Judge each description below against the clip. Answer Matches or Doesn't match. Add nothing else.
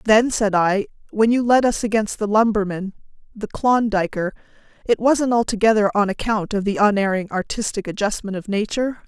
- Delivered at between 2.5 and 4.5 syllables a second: Doesn't match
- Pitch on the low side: Doesn't match